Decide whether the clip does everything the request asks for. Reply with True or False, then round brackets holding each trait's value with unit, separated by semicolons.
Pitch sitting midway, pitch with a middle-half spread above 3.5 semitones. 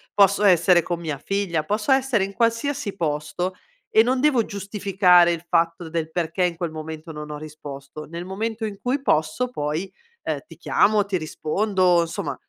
True (180 Hz; 4.4 semitones)